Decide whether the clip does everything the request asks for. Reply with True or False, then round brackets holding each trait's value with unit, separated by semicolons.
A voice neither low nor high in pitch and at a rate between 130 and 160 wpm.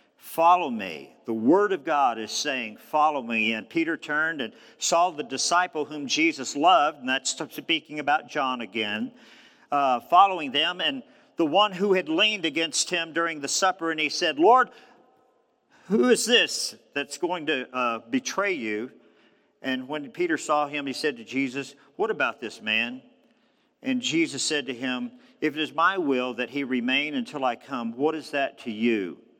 False (165 Hz; 180 wpm)